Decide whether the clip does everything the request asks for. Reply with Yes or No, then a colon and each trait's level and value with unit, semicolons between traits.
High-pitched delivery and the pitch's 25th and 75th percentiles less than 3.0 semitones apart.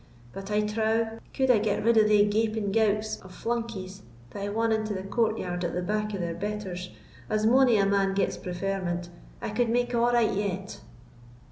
Yes: high, 210 Hz; narrow, 2.4 semitones